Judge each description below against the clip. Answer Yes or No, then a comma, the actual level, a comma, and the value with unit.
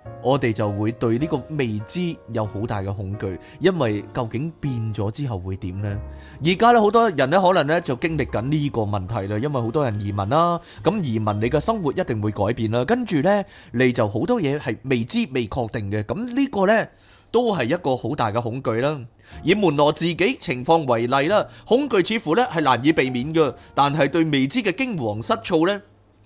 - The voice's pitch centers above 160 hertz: No, low, 130 Hz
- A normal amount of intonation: No, wide, 6.8 semitones